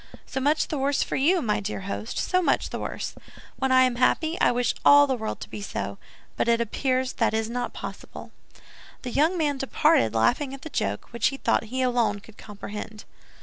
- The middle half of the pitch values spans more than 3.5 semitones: Yes, average, 4.2 semitones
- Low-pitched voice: No, very high, 255 Hz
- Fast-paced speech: Yes, fast, 210 wpm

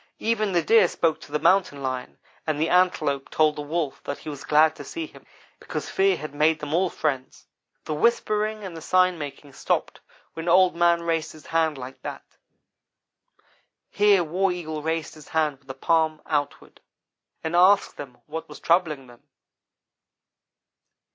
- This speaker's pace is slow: No, average, 170 wpm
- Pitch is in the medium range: Yes, medium, 160 Hz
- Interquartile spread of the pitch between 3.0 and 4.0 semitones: Yes, average, 3.4 semitones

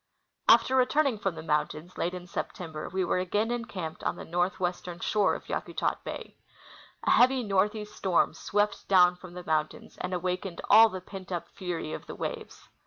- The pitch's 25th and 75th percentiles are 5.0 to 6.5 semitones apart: No, average, 3.0 semitones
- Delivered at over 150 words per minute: Yes, average, 175 wpm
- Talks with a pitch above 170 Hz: Yes, medium, 185 Hz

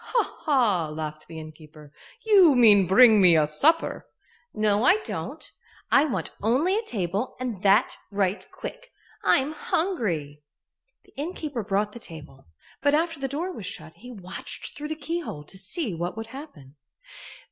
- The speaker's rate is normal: Yes, average, 160 wpm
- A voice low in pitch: No, high, 215 Hz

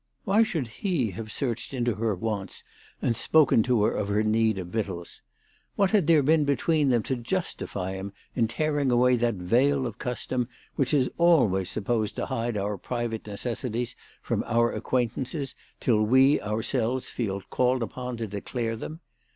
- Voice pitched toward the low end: Yes, low, 120 Hz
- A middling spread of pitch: Yes, average, 3.6 semitones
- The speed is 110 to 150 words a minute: No, average, 165 wpm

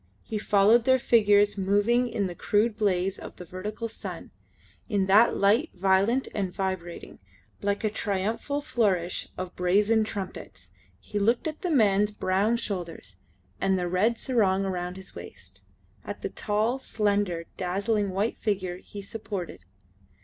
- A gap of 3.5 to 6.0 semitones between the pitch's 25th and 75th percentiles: No, average, 2.9 semitones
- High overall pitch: Yes, high, 205 Hz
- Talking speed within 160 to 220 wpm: No, average, 145 wpm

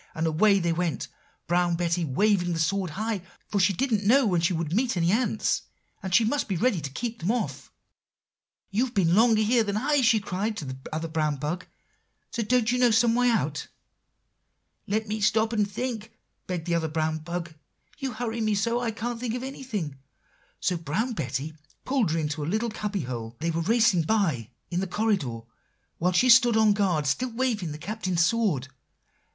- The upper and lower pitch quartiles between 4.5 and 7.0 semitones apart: Yes, wide, 5.5 semitones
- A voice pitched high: Yes, high, 200 Hz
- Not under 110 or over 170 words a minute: No, average, 190 wpm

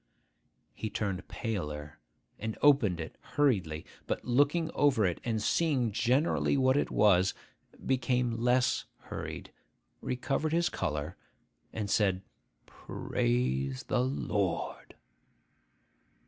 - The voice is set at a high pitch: No, low, 110 Hz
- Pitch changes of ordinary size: No, wide, 6.3 semitones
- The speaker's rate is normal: No, slow, 105 wpm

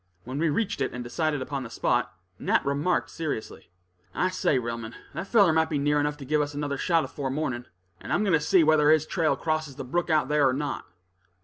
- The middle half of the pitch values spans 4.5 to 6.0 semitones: No, average, 2.7 semitones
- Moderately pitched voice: Yes, medium, 150 Hz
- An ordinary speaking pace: No, fast, 225 wpm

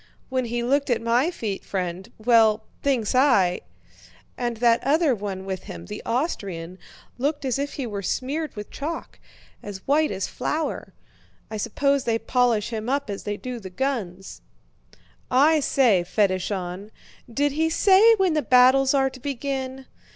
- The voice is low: No, high, 245 Hz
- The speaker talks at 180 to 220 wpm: No, average, 155 wpm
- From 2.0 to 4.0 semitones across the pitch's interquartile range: No, wide, 5.4 semitones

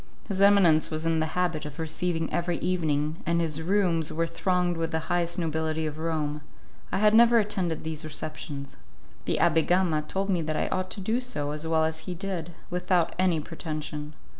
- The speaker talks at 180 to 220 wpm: Yes, average, 190 wpm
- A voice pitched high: No, medium, 165 Hz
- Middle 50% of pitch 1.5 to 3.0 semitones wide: Yes, narrow, 2.5 semitones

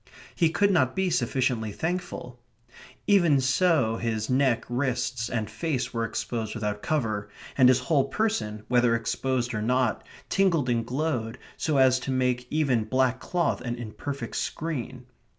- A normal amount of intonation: Yes, average, 4.3 semitones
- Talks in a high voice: No, low, 125 Hz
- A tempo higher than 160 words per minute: No, average, 150 wpm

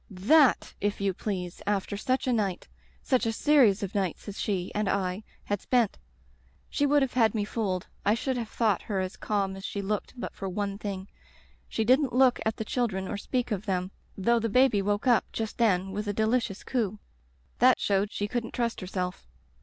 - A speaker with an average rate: No, fast, 215 wpm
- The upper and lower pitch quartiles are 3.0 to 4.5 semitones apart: Yes, average, 3.5 semitones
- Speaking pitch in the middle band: No, high, 210 Hz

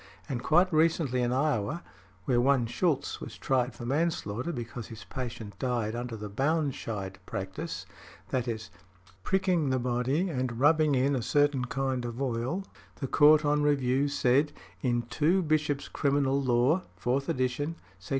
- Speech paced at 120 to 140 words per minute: No, average, 150 wpm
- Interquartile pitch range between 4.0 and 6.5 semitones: No, average, 3.6 semitones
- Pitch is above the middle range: No, low, 130 Hz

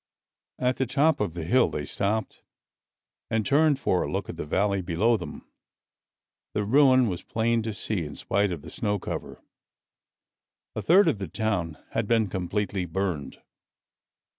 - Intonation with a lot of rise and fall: No, average, 4.7 semitones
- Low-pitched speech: Yes, low, 105 Hz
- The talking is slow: No, average, 165 wpm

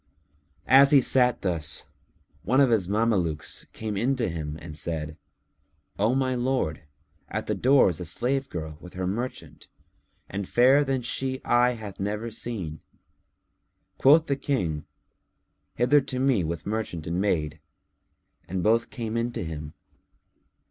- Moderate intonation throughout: No, wide, 7.1 semitones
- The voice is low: Yes, low, 110 Hz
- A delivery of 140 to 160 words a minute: Yes, average, 150 wpm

